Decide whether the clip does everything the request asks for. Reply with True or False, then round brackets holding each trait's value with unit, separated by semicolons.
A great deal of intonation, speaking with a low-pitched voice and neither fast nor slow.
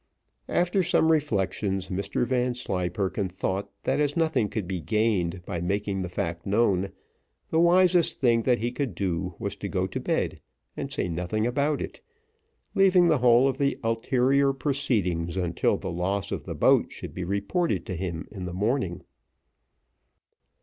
True (6.8 semitones; 105 Hz; 160 wpm)